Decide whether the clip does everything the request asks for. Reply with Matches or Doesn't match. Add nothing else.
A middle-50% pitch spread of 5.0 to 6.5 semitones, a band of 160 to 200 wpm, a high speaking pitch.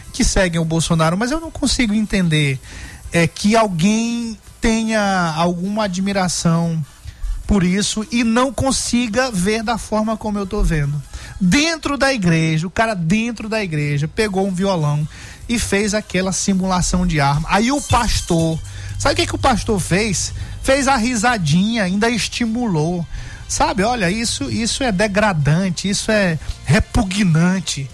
Doesn't match